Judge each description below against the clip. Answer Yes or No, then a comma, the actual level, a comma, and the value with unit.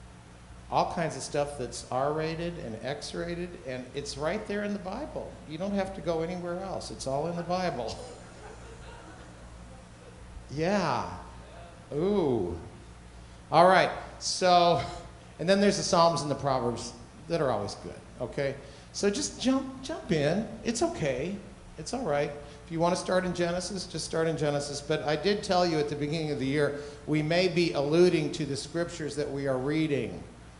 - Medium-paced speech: Yes, average, 175 wpm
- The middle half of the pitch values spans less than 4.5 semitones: No, average, 4.9 semitones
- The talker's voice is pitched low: No, medium, 150 Hz